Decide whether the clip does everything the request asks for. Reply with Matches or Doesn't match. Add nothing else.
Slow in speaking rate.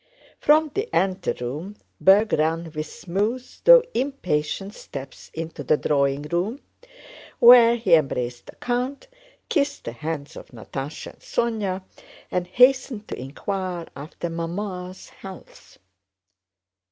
Matches